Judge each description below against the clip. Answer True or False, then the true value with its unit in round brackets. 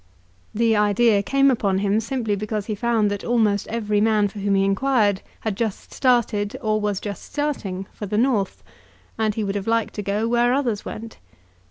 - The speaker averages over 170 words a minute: True (190 wpm)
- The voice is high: True (215 Hz)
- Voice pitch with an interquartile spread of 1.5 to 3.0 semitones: True (2.4 semitones)